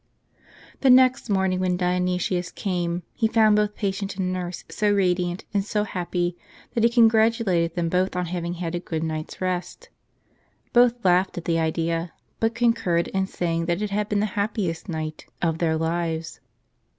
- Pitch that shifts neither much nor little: Yes, average, 3.5 semitones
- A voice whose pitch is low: No, medium, 180 Hz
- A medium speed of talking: Yes, average, 170 wpm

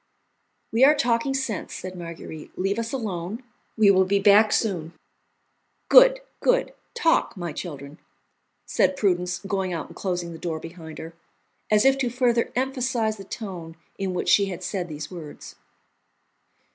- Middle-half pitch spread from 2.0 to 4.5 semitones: No, average, 5.2 semitones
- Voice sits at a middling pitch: No, high, 195 Hz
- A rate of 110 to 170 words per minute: Yes, average, 155 wpm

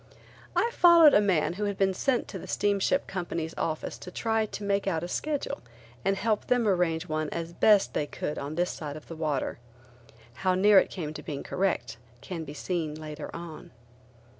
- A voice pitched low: No, medium, 180 Hz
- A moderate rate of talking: Yes, average, 195 wpm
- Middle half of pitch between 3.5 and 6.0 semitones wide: Yes, average, 4.6 semitones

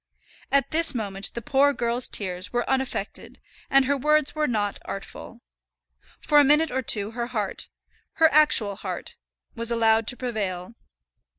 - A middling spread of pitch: Yes, average, 5.0 semitones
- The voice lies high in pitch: Yes, high, 240 Hz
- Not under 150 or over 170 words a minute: Yes, average, 155 wpm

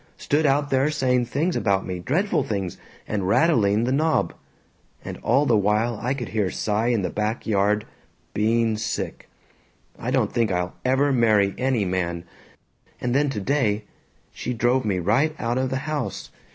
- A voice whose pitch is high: No, low, 115 Hz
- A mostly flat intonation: No, average, 4.4 semitones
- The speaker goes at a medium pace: Yes, average, 165 wpm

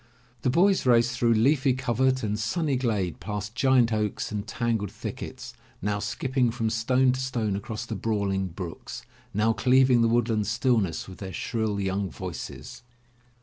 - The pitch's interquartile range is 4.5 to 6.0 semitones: No, average, 3.7 semitones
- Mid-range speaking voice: No, low, 115 Hz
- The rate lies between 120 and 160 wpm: Yes, average, 155 wpm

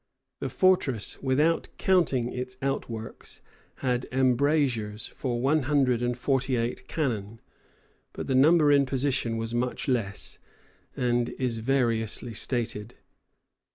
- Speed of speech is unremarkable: No, slow, 120 wpm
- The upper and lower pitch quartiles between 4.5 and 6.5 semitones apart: No, average, 2.8 semitones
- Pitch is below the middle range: Yes, low, 125 Hz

